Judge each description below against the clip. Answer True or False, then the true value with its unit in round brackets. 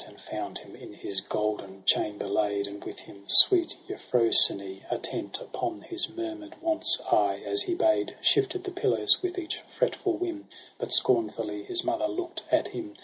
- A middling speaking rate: True (165 wpm)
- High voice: True (330 Hz)